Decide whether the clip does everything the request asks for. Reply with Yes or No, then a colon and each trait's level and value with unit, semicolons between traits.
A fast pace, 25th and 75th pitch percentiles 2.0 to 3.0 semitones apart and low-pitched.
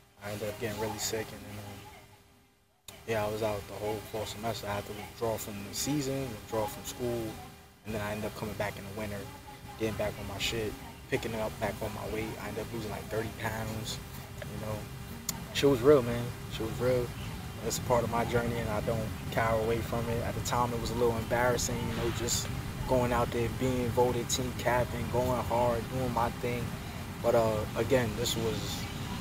Yes: fast, 220 wpm; narrow, 2.4 semitones; low, 115 Hz